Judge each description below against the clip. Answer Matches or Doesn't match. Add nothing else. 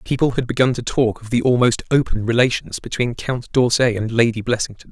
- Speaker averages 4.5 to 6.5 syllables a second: Matches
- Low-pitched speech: Matches